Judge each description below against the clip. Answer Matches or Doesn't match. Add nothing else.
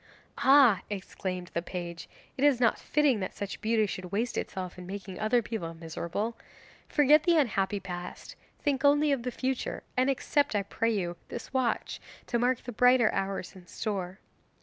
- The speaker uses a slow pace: Doesn't match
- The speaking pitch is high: Matches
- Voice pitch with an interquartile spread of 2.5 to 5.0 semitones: Doesn't match